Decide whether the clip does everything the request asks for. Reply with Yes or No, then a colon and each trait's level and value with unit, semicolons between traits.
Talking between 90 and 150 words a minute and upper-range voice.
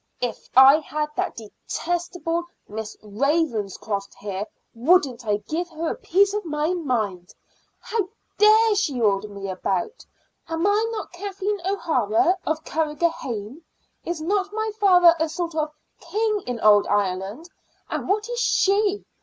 Yes: average, 140 wpm; very high, 320 Hz